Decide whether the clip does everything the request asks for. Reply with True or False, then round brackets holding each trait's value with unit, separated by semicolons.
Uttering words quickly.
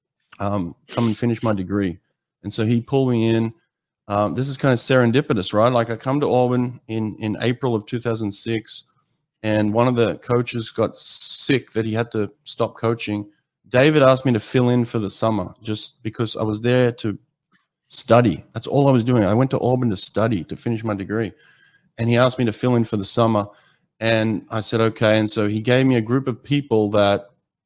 True (210 wpm)